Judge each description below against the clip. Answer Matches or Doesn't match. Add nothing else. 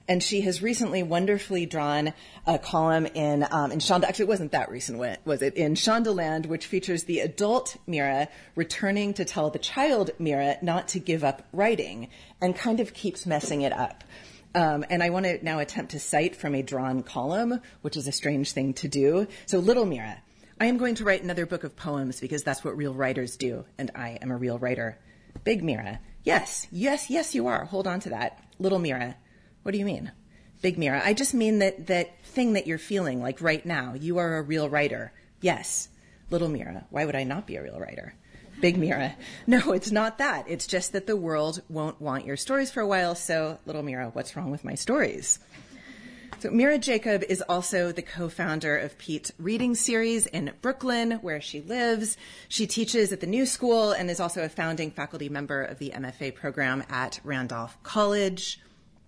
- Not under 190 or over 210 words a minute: Matches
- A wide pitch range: Matches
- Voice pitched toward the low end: Doesn't match